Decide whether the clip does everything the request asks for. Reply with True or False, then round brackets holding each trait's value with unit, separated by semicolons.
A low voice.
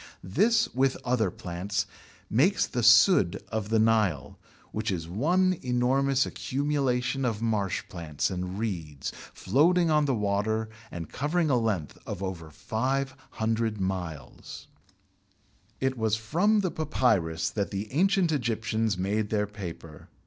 True (110 Hz)